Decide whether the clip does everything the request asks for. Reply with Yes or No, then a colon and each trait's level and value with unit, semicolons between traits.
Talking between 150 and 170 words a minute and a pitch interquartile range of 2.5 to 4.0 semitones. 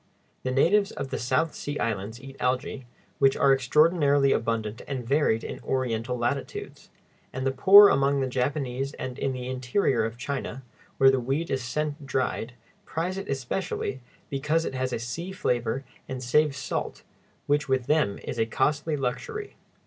Yes: average, 165 wpm; average, 2.9 semitones